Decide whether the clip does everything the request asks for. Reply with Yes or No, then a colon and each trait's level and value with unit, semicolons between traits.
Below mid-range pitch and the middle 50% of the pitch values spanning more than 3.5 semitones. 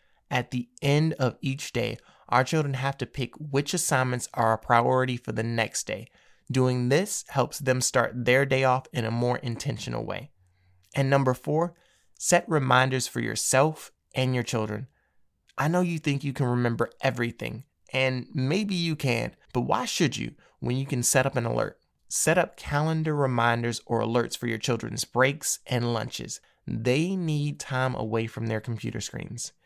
No: low, 130 Hz; average, 3.0 semitones